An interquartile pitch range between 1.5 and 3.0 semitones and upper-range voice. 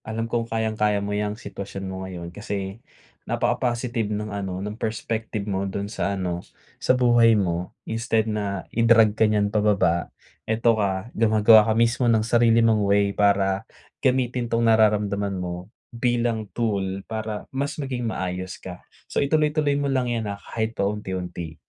No: average, 2.7 semitones; low, 105 Hz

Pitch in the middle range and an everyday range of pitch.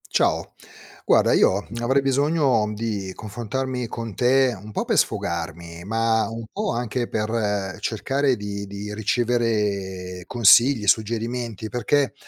No: low, 110 Hz; average, 3.4 semitones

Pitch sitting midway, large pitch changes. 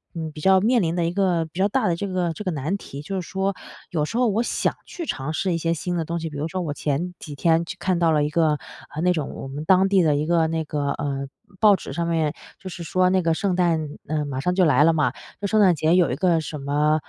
No: medium, 165 Hz; average, 3.4 semitones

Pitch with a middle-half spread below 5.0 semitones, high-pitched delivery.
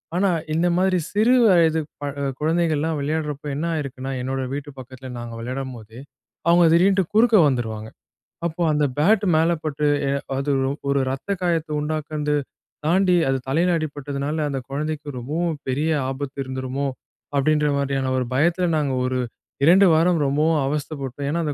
No: average, 3.4 semitones; medium, 150 Hz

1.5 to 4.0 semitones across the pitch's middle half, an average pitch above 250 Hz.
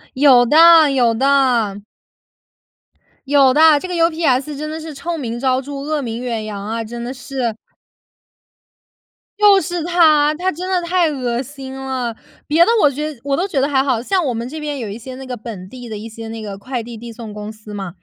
No: average, 4.8 semitones; very high, 265 Hz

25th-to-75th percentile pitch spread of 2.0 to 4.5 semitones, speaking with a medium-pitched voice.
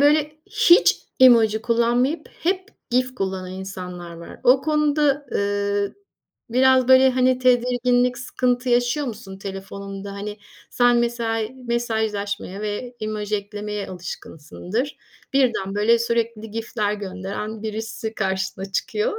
No: average, 3.7 semitones; high, 225 Hz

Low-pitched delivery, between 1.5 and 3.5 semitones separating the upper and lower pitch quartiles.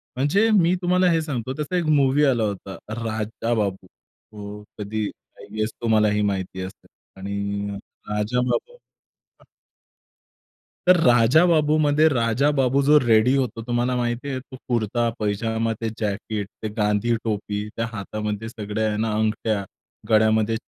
No: low, 115 Hz; average, 4.0 semitones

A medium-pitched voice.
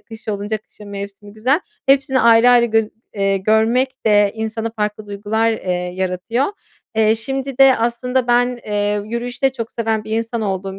No: high, 220 Hz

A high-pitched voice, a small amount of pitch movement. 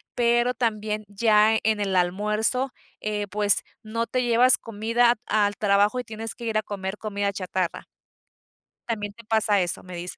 Yes: high, 215 Hz; narrow, 2.2 semitones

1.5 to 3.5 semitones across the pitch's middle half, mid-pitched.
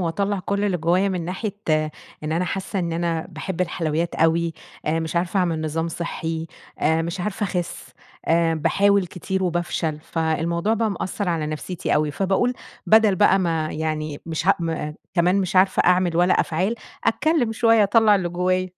Yes: average, 2.9 semitones; medium, 175 Hz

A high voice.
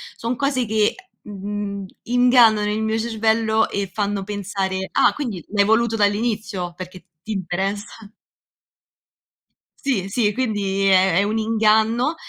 Yes: high, 210 Hz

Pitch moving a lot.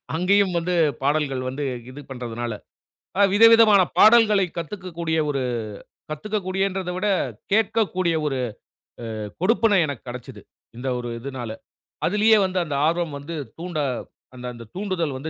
Yes: wide, 6.4 semitones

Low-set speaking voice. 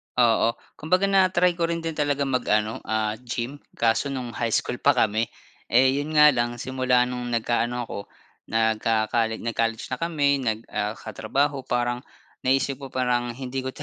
Yes: low, 125 Hz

